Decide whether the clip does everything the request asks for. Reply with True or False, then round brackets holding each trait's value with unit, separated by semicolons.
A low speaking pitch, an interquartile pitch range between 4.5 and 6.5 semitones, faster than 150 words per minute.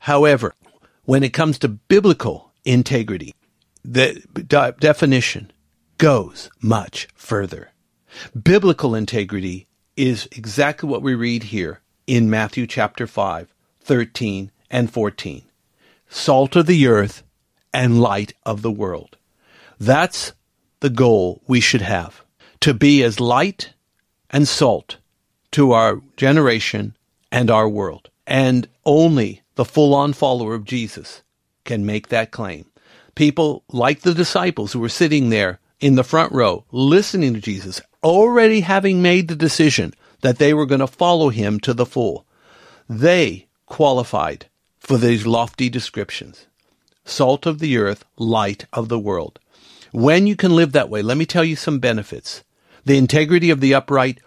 False (130 Hz; 5.2 semitones; 140 wpm)